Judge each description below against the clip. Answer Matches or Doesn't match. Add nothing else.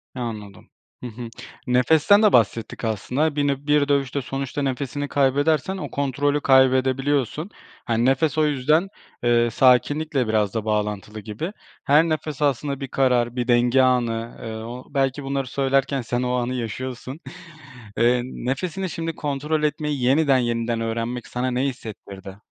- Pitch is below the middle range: Matches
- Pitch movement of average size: Matches